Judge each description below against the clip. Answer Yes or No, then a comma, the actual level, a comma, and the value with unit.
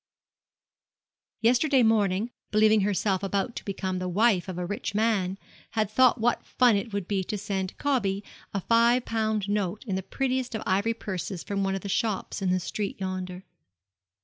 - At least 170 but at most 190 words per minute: Yes, average, 180 wpm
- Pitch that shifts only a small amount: No, average, 3.0 semitones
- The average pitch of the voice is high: Yes, high, 205 Hz